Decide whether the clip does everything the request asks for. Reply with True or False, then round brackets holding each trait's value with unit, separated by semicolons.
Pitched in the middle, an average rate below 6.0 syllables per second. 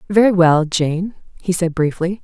True (175 Hz; 4.5 syllables/s)